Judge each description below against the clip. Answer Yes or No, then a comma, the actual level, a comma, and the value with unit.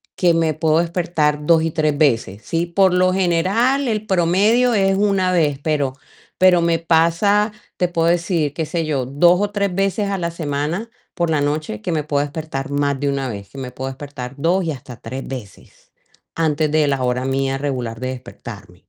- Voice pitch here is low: No, medium, 160 Hz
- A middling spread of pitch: Yes, average, 4.3 semitones